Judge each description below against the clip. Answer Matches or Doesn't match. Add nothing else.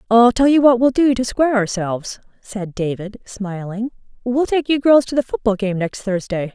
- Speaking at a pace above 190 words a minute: Matches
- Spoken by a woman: Matches